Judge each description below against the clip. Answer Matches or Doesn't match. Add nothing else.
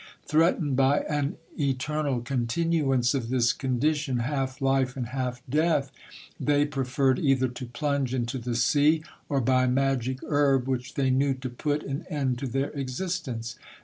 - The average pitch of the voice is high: Doesn't match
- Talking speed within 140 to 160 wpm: Matches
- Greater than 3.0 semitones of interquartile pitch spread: Doesn't match